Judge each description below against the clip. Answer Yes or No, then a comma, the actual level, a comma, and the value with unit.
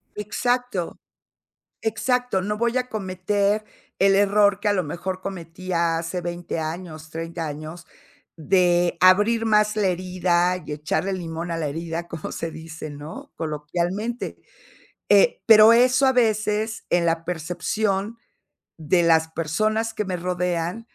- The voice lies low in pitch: No, medium, 185 Hz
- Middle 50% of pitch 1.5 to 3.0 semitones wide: No, average, 4.2 semitones